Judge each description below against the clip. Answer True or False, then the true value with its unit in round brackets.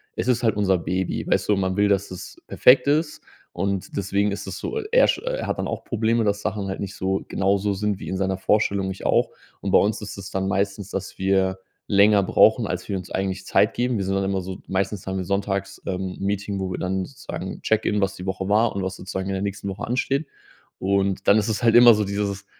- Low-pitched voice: True (100 Hz)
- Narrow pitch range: True (1.5 semitones)